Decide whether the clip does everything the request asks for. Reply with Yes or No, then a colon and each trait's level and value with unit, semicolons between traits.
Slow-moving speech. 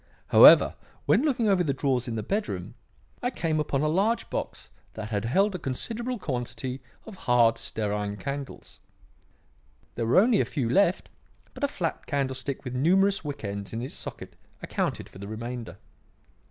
No: average, 165 wpm